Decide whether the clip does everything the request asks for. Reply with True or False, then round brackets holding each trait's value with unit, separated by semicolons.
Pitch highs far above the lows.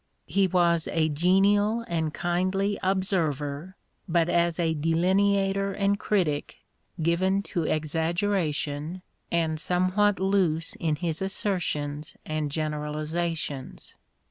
False (3.7 semitones)